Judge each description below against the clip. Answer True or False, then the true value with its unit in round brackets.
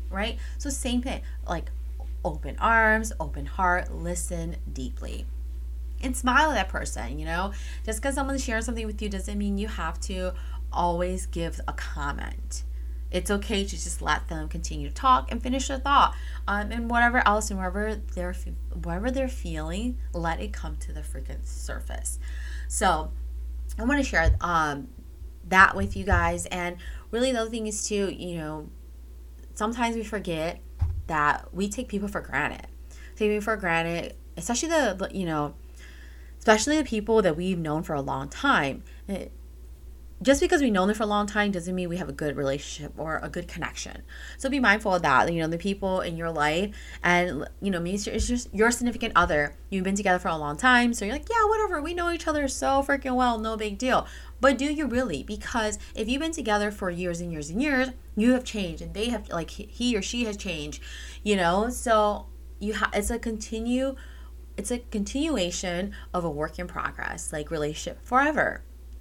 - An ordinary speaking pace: True (190 wpm)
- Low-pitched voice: False (180 Hz)